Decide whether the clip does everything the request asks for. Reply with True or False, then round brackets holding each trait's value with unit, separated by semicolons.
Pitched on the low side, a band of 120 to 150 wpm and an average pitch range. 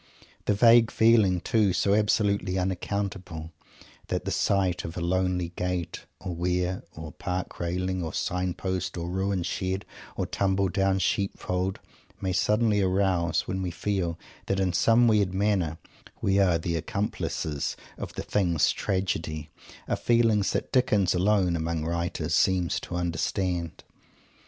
False (95 Hz; 145 wpm; 2.3 semitones)